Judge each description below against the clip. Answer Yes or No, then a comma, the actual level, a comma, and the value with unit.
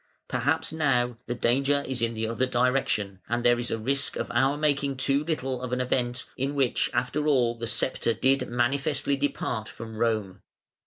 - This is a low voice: Yes, low, 125 Hz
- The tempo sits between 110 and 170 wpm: No, average, 180 wpm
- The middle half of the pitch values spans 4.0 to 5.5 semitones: No, average, 2.8 semitones